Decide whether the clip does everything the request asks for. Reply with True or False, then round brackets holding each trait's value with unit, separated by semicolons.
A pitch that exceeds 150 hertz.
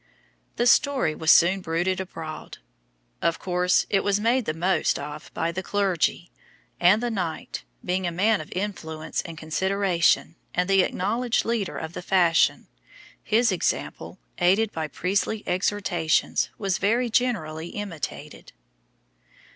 True (185 Hz)